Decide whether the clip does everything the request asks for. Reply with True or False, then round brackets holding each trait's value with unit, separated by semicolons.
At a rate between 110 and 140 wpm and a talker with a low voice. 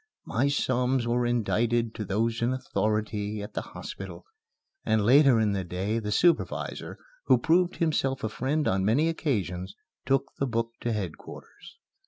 False (155 wpm; 115 Hz)